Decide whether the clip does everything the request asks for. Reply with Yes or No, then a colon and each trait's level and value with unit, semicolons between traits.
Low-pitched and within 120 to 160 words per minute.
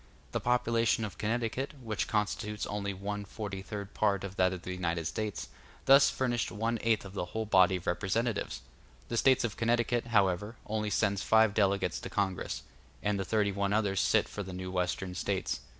No: low, 105 Hz; average, 185 wpm